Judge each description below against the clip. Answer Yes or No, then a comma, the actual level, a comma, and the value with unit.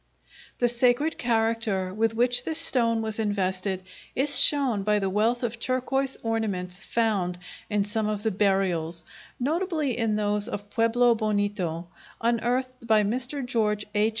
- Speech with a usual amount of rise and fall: Yes, average, 3.1 semitones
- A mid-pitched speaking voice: No, high, 225 Hz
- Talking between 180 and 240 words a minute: No, average, 145 wpm